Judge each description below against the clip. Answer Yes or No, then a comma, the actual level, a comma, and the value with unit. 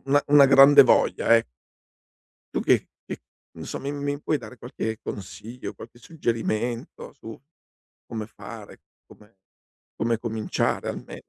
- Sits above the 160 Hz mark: No, low, 120 Hz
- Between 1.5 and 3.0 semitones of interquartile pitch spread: No, average, 3.9 semitones